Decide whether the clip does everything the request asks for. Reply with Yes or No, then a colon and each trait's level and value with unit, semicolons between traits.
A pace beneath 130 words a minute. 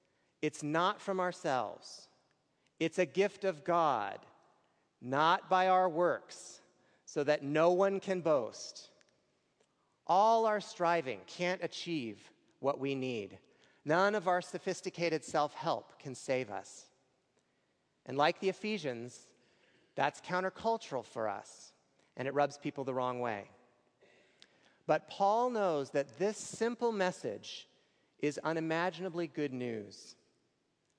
Yes: slow, 120 wpm